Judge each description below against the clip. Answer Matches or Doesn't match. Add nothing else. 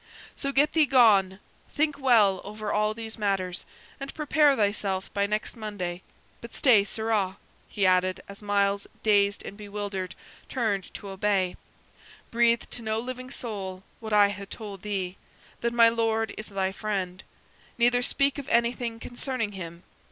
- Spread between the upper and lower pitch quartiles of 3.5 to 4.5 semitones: Doesn't match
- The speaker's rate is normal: Matches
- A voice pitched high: Matches